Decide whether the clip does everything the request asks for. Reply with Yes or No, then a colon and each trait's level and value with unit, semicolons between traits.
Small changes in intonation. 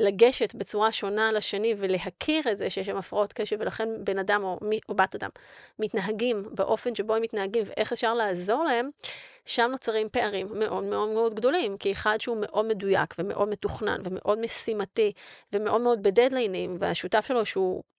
Yes: narrow, 2.1 semitones